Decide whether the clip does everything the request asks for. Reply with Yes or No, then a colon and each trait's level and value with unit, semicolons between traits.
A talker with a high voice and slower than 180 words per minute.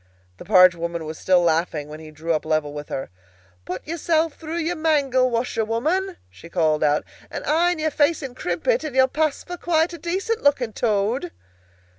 No: very high, 255 Hz; average, 190 wpm